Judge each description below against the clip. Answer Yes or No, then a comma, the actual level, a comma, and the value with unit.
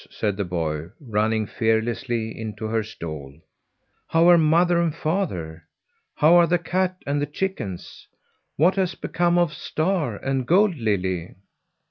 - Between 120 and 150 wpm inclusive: Yes, average, 140 wpm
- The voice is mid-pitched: No, low, 130 Hz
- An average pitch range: No, wide, 8.7 semitones